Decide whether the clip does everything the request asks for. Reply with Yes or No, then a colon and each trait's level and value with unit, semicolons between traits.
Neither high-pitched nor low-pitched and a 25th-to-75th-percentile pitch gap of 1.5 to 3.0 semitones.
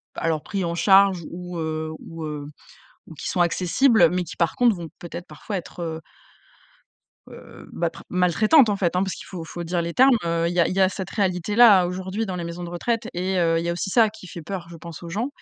Yes: medium, 180 Hz; narrow, 2.4 semitones